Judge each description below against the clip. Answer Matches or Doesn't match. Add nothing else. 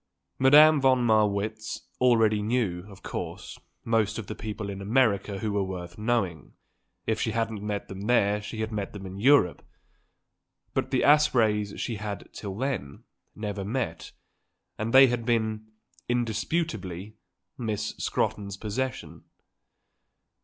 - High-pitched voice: Doesn't match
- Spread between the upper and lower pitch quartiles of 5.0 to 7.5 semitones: Doesn't match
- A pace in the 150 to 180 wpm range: Doesn't match